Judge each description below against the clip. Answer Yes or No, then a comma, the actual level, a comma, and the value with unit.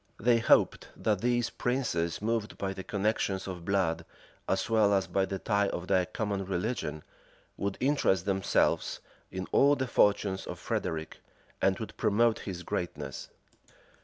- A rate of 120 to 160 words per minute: Yes, average, 150 wpm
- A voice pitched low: Yes, low, 100 Hz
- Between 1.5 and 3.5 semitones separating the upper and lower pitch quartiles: Yes, average, 3.2 semitones